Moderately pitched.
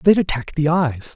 Yes: medium, 155 Hz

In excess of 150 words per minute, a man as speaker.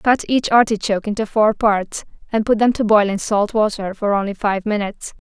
No: fast, 205 wpm; female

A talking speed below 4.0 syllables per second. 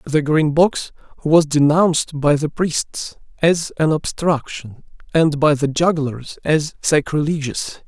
Yes: 3.7 syllables/s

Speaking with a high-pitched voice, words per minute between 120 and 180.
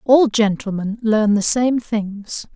Yes: high, 220 Hz; average, 140 wpm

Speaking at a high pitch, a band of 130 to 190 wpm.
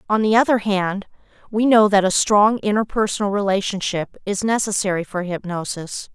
Yes: high, 205 Hz; average, 145 wpm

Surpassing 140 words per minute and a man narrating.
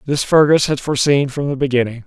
Yes: fast, 205 wpm; male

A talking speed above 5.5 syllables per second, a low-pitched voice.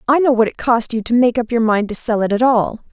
No: 6.0 syllables/s; high, 230 Hz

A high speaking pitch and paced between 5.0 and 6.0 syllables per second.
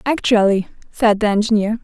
Yes: high, 215 Hz; 5.3 syllables/s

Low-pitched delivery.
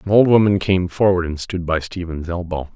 Yes: very low, 90 Hz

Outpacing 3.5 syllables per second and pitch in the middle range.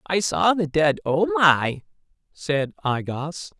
No: 3.3 syllables/s; medium, 150 Hz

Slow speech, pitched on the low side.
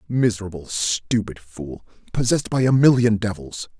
Yes: slow, 125 wpm; low, 110 Hz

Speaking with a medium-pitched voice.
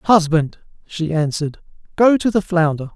Yes: medium, 170 Hz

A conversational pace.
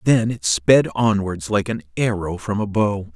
Yes: average, 190 wpm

